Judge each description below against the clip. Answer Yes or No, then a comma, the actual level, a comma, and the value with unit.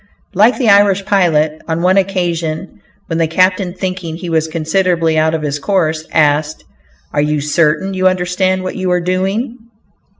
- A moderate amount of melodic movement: Yes, average, 3.0 semitones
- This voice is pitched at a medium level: Yes, medium, 175 Hz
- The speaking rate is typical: Yes, average, 165 wpm